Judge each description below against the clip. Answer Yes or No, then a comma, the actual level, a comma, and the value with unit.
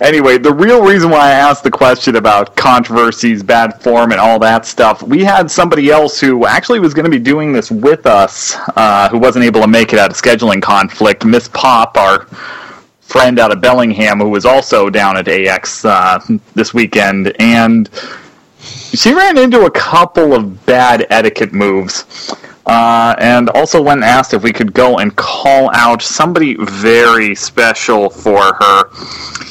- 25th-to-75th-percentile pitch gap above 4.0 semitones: Yes, average, 4.6 semitones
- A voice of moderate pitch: No, low, 120 Hz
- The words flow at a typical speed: Yes, average, 175 wpm